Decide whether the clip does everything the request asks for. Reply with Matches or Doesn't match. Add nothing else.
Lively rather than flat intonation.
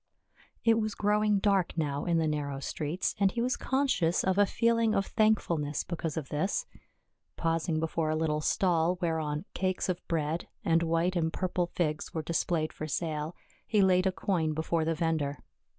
Doesn't match